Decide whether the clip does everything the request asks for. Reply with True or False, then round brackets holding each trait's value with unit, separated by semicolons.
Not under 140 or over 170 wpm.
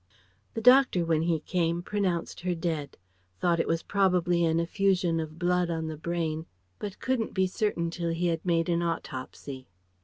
False (180 wpm)